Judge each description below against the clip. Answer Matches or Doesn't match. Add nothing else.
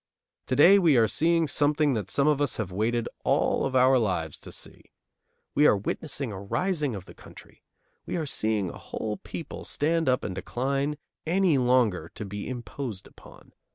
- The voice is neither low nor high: Doesn't match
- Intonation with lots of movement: Matches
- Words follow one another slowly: Doesn't match